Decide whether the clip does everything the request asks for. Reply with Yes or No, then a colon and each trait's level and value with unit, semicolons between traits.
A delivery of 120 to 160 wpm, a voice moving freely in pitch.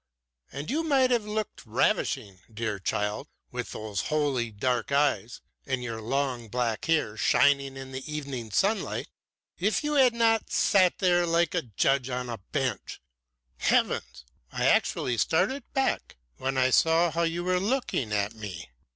Yes: average, 155 wpm; wide, 7.4 semitones